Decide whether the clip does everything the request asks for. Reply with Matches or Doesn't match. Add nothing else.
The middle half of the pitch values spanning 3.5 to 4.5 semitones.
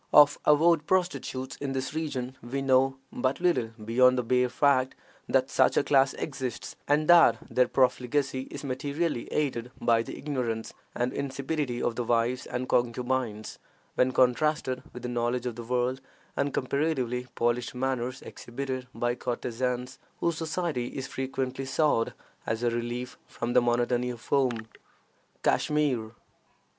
Doesn't match